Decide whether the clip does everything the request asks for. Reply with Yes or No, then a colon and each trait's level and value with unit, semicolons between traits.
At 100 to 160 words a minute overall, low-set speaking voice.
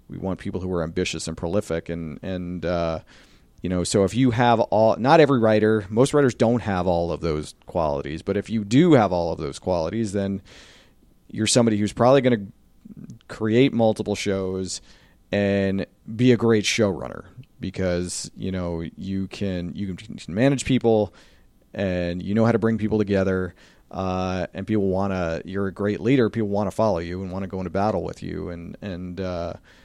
No: average, 190 wpm; low, 100 Hz